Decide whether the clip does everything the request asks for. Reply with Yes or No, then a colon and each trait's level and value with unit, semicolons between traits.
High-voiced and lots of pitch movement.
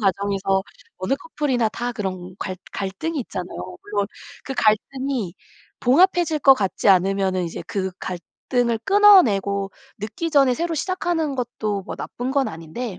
Yes: high, 220 Hz; wide, 6.2 semitones